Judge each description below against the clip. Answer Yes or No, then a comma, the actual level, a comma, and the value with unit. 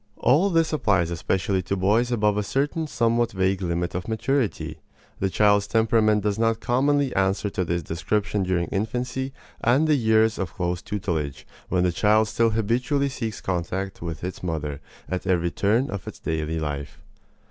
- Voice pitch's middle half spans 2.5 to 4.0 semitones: No, average, 4.7 semitones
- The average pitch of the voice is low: Yes, low, 100 Hz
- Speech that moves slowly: No, average, 170 wpm